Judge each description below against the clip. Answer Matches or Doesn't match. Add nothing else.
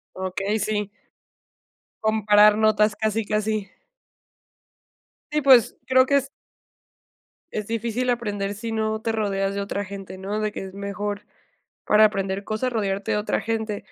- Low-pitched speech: Doesn't match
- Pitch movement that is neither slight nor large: Doesn't match